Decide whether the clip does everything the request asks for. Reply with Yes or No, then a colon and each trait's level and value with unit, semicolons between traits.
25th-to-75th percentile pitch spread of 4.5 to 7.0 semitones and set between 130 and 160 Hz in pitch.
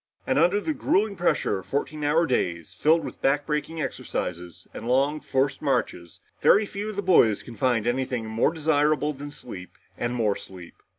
Yes: wide, 5.6 semitones; medium, 140 Hz